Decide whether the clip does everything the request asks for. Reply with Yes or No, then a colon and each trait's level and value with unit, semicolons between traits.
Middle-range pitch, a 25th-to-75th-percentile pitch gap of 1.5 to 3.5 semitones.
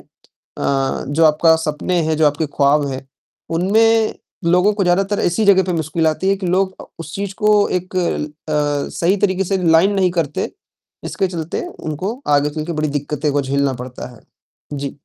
No: medium, 165 Hz; average, 4.3 semitones